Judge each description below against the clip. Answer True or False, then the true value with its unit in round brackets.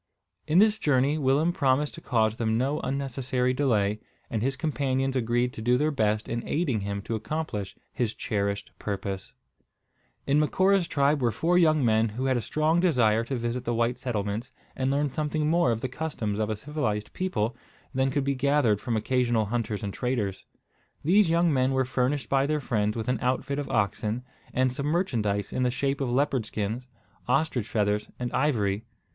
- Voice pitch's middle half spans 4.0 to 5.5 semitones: True (4.5 semitones)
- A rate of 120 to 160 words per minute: False (185 wpm)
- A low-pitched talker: True (125 Hz)